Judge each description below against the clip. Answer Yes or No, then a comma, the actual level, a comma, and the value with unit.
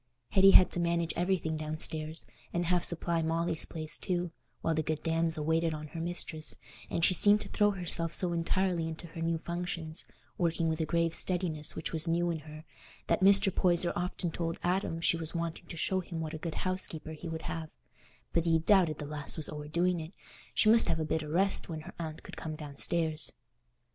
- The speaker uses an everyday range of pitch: No, narrow, 1.7 semitones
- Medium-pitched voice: Yes, medium, 165 Hz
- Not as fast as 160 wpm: No, fast, 205 wpm